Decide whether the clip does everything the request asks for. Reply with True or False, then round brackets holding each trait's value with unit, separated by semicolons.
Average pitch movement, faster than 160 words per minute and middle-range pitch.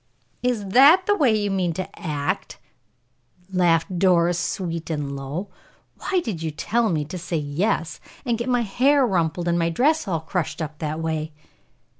False (5.7 semitones; 170 wpm; 175 Hz)